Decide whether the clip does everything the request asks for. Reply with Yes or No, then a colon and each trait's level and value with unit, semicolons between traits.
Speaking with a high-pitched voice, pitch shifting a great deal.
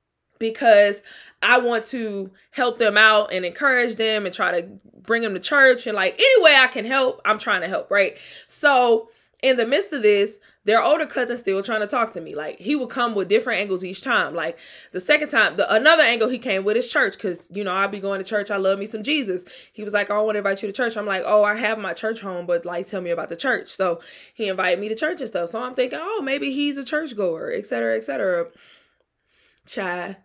No: high, 220 Hz; average, 4.6 semitones